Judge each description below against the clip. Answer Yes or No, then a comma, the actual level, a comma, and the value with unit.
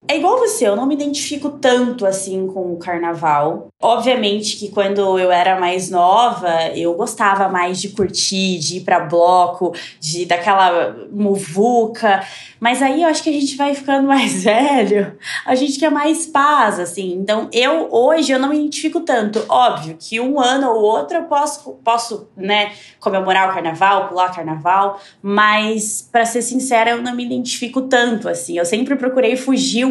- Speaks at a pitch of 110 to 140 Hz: No, high, 215 Hz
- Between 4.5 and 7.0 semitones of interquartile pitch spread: Yes, wide, 5.5 semitones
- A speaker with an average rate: Yes, average, 175 wpm